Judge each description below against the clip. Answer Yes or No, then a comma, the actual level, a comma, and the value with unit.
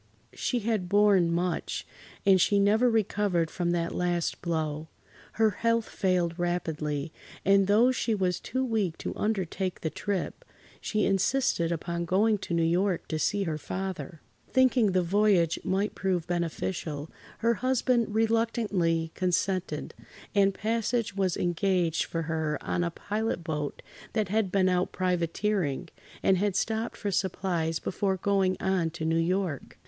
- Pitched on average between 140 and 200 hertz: Yes, medium, 185 Hz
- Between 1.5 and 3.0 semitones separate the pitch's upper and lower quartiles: No, average, 3.6 semitones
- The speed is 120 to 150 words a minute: Yes, average, 145 wpm